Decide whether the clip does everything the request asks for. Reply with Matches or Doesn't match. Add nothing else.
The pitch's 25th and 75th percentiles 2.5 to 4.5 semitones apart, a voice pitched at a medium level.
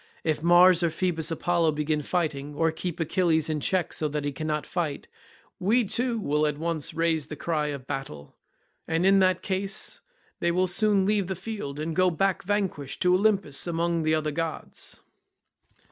Matches